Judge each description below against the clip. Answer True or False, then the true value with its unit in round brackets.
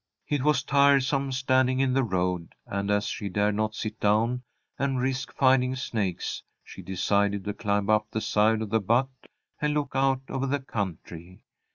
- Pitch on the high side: False (115 Hz)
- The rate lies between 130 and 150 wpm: False (175 wpm)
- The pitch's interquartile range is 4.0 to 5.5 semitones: True (4.7 semitones)